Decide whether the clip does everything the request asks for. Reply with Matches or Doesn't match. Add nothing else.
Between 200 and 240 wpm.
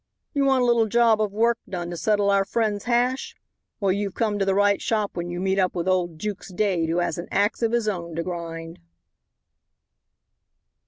Matches